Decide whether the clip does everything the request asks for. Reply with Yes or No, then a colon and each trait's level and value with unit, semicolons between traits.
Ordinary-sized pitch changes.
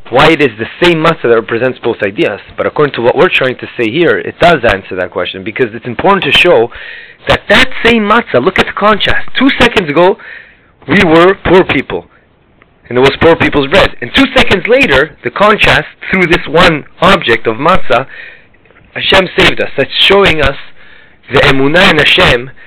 No: wide, 7.1 semitones